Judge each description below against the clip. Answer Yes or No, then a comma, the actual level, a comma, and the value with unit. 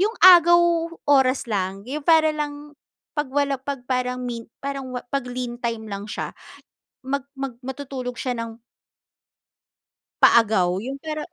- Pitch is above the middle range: Yes, very high, 265 Hz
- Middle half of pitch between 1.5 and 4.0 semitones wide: Yes, average, 3.5 semitones